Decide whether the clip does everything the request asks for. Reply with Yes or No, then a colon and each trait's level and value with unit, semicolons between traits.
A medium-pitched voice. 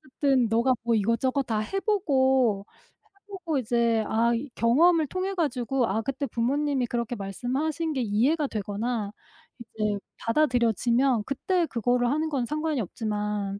No: high, 245 Hz